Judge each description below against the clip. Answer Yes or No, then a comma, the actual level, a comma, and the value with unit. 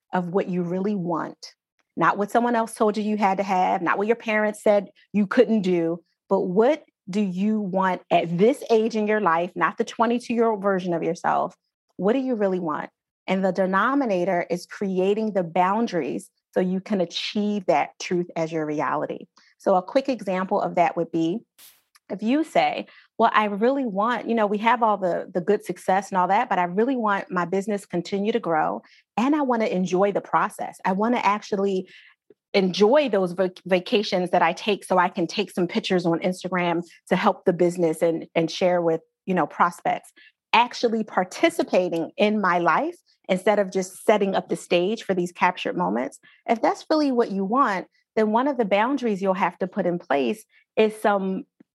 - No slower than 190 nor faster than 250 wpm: Yes, average, 200 wpm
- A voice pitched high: Yes, high, 200 Hz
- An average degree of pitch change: Yes, average, 3.7 semitones